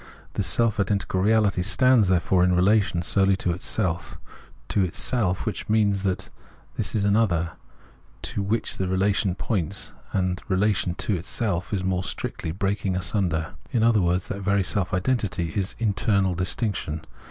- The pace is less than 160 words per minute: Yes, average, 150 wpm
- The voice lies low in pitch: Yes, very low, 95 Hz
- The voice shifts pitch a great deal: No, narrow, 2.5 semitones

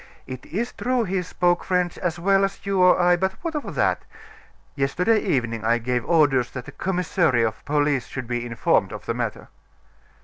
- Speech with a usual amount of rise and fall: No, wide, 7.0 semitones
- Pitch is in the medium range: Yes, medium, 175 Hz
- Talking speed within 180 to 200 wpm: Yes, average, 190 wpm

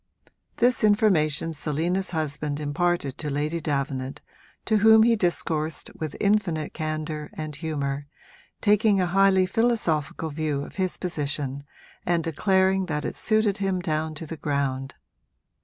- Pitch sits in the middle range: Yes, medium, 160 Hz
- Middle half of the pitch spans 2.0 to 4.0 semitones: No, average, 4.4 semitones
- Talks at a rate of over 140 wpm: No, slow, 135 wpm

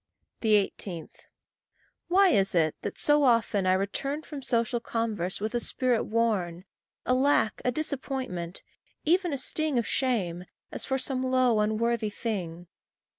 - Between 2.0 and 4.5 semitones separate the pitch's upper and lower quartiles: No, average, 5.1 semitones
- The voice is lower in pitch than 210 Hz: No, high, 230 Hz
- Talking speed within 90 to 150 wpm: Yes, average, 140 wpm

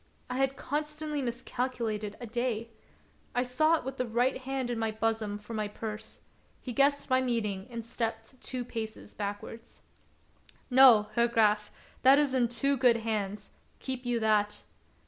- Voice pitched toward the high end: Yes, high, 235 Hz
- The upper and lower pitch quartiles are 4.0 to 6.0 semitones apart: No, average, 3.0 semitones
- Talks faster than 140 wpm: Yes, average, 155 wpm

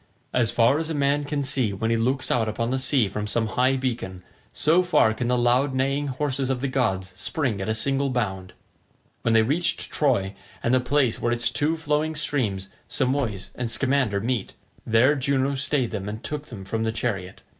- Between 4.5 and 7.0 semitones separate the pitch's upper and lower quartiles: No, average, 4.0 semitones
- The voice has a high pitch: No, low, 125 Hz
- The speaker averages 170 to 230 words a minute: Yes, average, 200 wpm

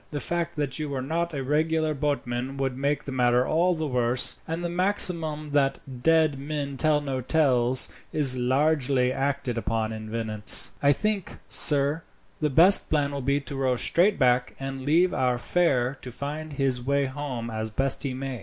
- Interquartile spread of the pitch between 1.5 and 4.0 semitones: Yes, average, 3.4 semitones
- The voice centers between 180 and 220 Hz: No, medium, 140 Hz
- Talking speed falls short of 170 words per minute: No, average, 180 wpm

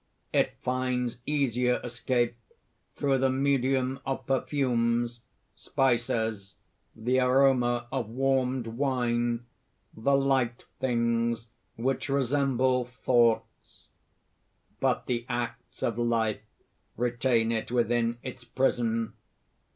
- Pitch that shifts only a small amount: Yes, narrow, 2.0 semitones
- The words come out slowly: Yes, slow, 95 wpm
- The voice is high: No, low, 125 Hz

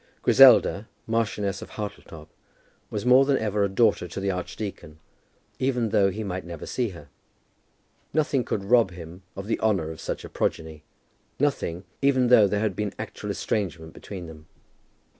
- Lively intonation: No, average, 4.5 semitones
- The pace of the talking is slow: No, average, 160 wpm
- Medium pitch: No, low, 100 Hz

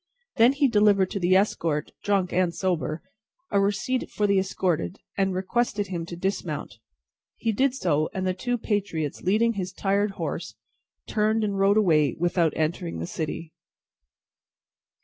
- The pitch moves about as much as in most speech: Yes, average, 3.5 semitones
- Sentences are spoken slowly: No, average, 150 wpm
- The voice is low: No, high, 190 Hz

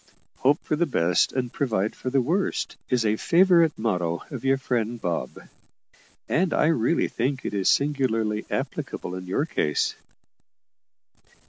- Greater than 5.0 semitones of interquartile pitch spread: Yes, wide, 5.6 semitones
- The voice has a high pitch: No, low, 125 Hz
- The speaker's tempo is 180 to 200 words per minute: No, average, 145 wpm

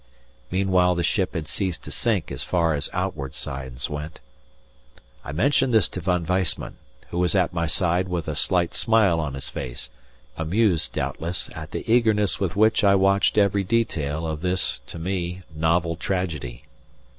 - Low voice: Yes, very low, 90 Hz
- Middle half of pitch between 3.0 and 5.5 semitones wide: Yes, average, 3.6 semitones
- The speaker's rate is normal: Yes, average, 170 wpm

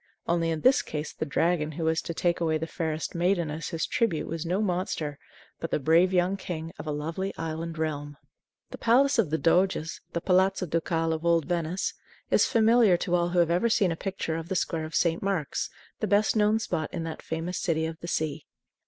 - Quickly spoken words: Yes, fast, 215 wpm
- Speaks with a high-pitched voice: No, medium, 170 Hz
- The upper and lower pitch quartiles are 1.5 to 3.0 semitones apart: Yes, narrow, 2.6 semitones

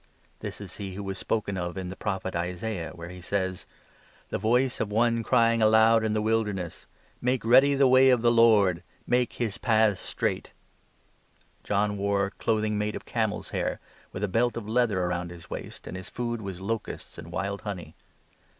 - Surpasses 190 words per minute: Yes, average, 200 wpm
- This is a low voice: Yes, low, 105 Hz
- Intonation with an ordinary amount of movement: Yes, average, 3.5 semitones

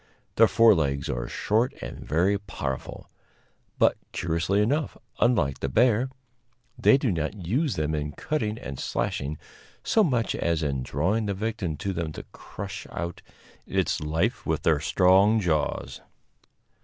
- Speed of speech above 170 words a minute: No, average, 145 wpm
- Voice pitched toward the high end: No, very low, 95 Hz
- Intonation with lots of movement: Yes, wide, 6.5 semitones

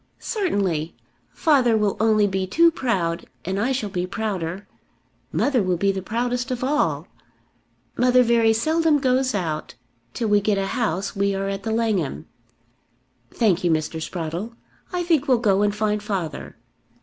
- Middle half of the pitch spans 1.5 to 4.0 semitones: No, average, 4.6 semitones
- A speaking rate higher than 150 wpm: Yes, average, 160 wpm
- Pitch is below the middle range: No, high, 210 Hz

